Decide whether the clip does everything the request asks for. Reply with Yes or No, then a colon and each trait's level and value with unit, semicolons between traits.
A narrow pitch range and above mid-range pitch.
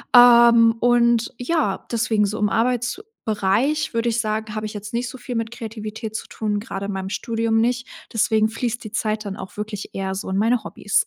Yes: narrow, 2.2 semitones; high, 225 Hz